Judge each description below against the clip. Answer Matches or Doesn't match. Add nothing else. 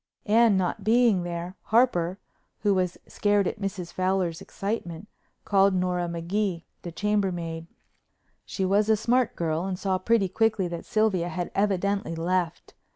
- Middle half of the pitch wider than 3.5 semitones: Doesn't match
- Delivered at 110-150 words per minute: Matches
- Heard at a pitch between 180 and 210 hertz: Matches